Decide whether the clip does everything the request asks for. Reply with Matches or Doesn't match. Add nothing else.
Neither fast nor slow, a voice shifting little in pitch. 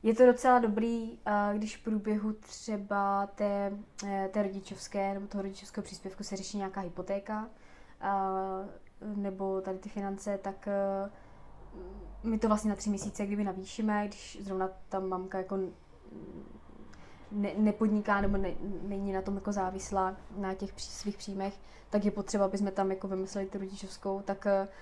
Matches